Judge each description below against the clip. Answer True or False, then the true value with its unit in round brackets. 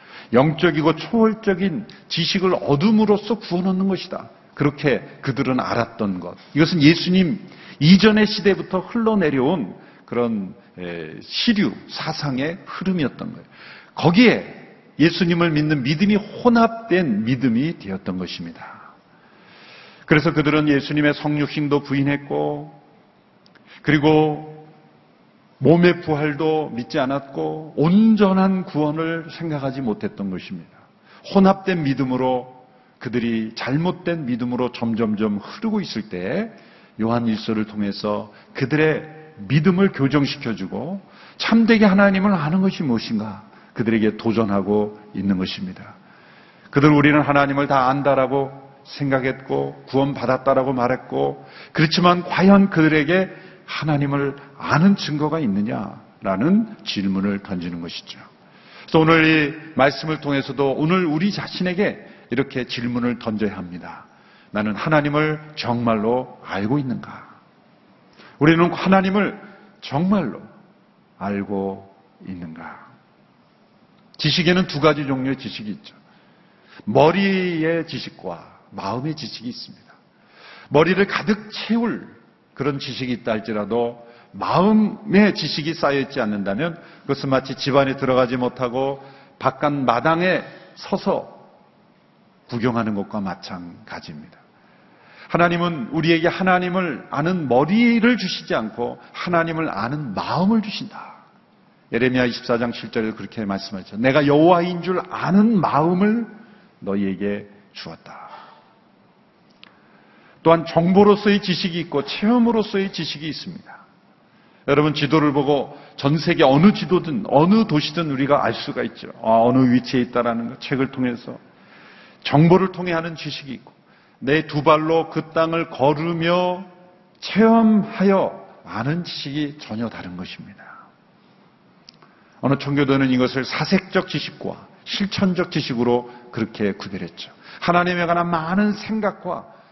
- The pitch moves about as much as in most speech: False (6.8 semitones)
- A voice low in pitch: False (150 Hz)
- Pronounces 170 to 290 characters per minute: True (280 characters per minute)